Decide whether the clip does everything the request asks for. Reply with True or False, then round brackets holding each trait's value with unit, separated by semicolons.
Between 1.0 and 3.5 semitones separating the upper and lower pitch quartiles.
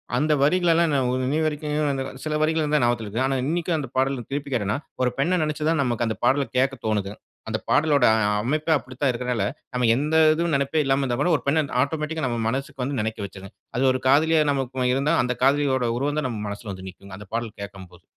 False (3.9 semitones)